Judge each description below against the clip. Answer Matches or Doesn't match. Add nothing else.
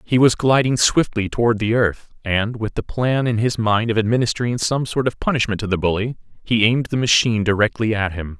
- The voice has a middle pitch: Doesn't match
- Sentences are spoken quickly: Matches